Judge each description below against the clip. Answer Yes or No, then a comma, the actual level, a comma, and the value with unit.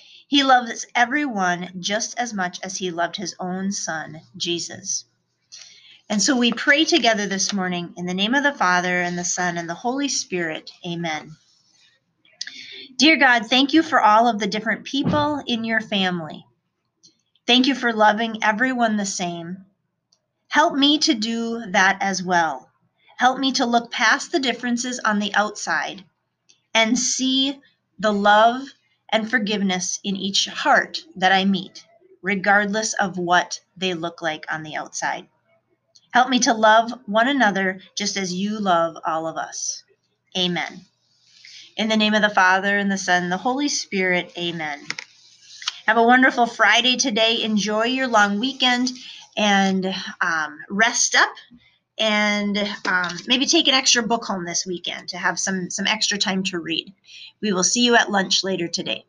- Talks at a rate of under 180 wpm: Yes, average, 160 wpm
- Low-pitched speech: No, high, 205 Hz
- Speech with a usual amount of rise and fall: Yes, average, 4.9 semitones